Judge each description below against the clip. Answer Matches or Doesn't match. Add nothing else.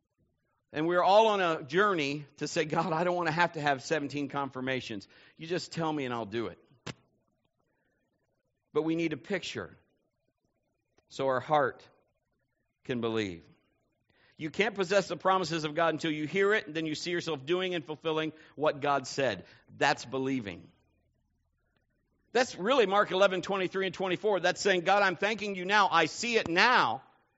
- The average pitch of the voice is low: Doesn't match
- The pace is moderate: Matches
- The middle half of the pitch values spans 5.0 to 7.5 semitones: Matches